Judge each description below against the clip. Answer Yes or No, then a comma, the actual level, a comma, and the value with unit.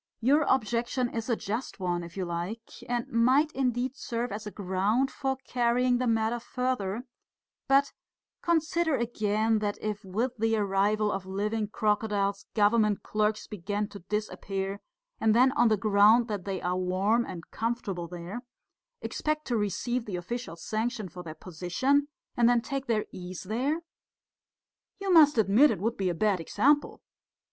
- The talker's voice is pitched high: Yes, high, 220 Hz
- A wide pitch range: No, average, 3.7 semitones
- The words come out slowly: No, average, 160 wpm